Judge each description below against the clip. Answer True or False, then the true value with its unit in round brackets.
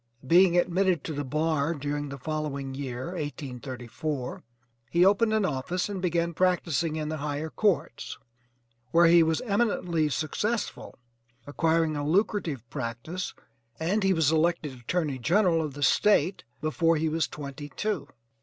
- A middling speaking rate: True (145 wpm)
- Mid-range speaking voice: True (160 Hz)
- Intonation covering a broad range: False (3.7 semitones)